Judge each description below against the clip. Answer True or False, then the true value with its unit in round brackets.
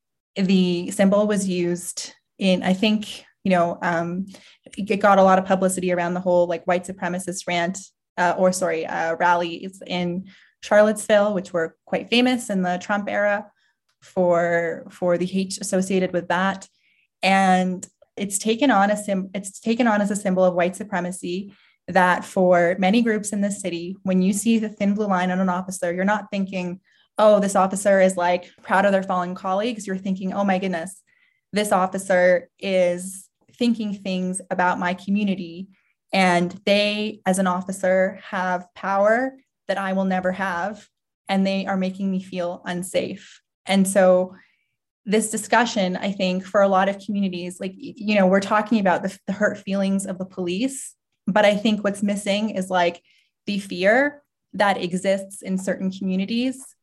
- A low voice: False (190 Hz)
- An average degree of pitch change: False (2.2 semitones)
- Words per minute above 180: False (170 wpm)